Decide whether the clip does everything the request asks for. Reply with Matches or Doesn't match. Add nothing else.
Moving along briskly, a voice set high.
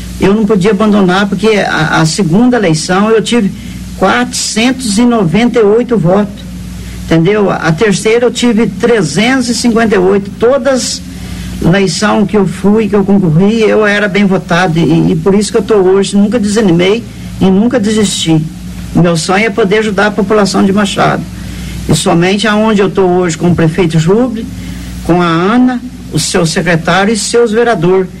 Doesn't match